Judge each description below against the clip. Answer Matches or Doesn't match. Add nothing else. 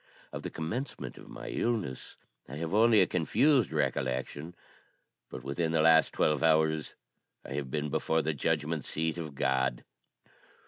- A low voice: Matches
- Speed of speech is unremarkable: Matches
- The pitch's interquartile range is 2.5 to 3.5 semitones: Matches